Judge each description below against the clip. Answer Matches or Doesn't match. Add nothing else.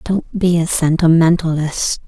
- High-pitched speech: Doesn't match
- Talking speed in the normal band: Doesn't match